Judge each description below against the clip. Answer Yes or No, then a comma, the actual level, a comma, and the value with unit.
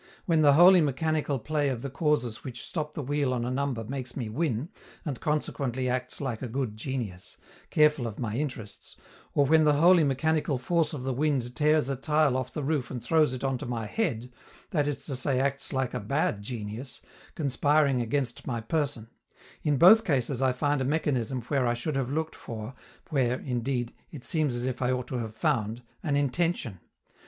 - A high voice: No, low, 135 Hz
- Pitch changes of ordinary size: Yes, average, 3.5 semitones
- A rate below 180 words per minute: No, average, 200 wpm